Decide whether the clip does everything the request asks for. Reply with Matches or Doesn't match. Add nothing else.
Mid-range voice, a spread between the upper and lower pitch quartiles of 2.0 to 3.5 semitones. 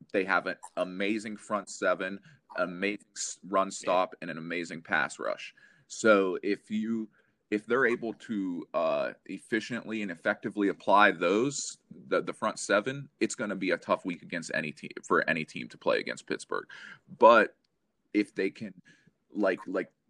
Doesn't match